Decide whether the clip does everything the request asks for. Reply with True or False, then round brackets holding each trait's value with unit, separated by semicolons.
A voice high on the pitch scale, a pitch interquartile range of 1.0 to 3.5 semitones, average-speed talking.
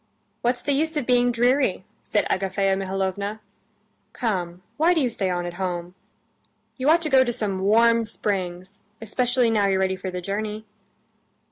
False (210 Hz; 4.6 semitones; 165 wpm)